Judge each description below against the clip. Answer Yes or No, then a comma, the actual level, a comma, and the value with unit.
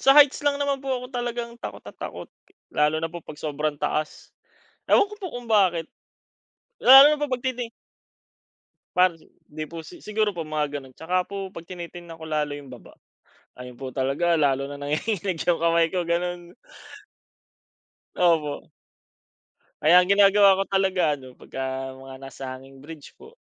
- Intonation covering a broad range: Yes, wide, 5.8 semitones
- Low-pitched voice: No, medium, 170 Hz